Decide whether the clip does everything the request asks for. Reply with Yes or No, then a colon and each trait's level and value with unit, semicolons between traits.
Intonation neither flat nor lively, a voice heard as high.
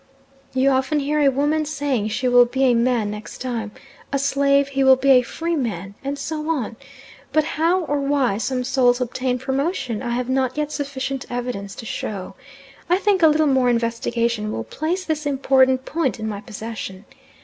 Yes: average, 3.3 semitones; very high, 260 Hz